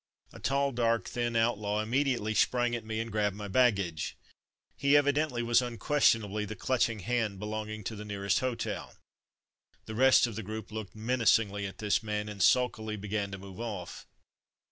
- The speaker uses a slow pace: No, average, 175 wpm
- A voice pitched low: Yes, low, 110 Hz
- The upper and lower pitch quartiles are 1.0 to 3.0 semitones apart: Yes, narrow, 2.6 semitones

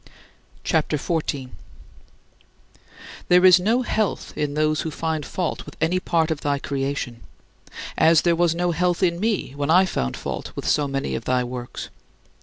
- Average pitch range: Yes, average, 3.9 semitones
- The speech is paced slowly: No, average, 170 wpm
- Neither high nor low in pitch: Yes, medium, 160 Hz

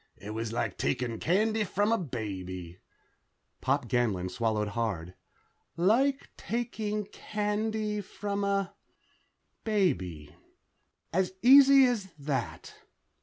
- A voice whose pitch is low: No, medium, 180 Hz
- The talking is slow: Yes, slow, 100 wpm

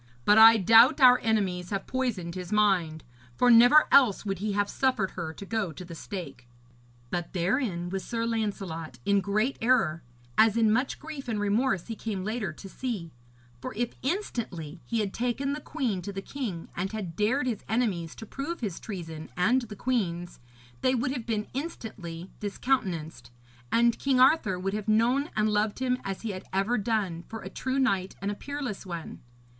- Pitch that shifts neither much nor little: Yes, average, 4.8 semitones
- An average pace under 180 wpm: No, average, 185 wpm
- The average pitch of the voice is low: No, high, 210 Hz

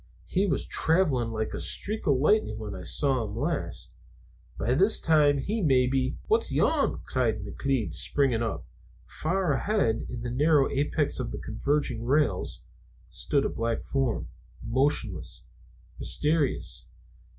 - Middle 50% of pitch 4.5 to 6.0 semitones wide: Yes, average, 4.9 semitones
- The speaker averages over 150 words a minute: No, average, 145 wpm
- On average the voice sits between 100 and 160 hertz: Yes, low, 135 Hz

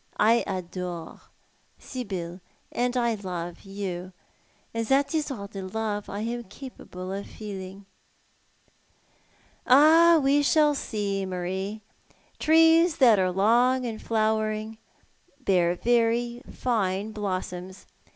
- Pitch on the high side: Yes, high, 215 Hz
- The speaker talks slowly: Yes, slow, 110 wpm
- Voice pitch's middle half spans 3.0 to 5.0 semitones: Yes, average, 4.4 semitones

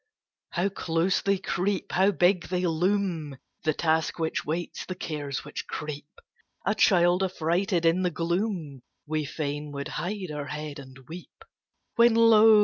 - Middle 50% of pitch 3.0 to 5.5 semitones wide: Yes, average, 3.8 semitones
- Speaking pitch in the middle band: Yes, medium, 170 Hz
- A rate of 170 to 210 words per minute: No, average, 150 wpm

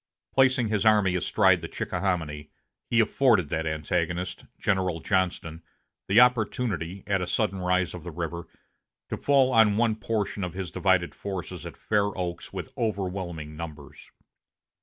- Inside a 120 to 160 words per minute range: Yes, average, 145 wpm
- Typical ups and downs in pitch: Yes, average, 3.8 semitones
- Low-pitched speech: Yes, very low, 95 Hz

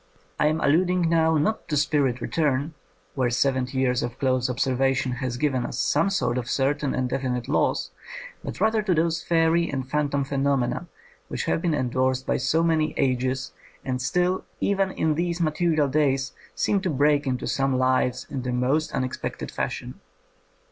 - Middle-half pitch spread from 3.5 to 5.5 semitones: Yes, average, 3.9 semitones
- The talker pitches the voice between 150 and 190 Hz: No, medium, 140 Hz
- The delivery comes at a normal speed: Yes, average, 170 wpm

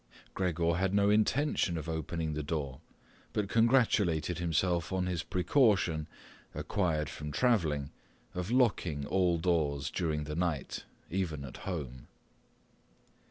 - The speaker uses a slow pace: Yes, slow, 120 wpm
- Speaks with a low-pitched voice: Yes, very low, 85 Hz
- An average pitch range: Yes, average, 3.9 semitones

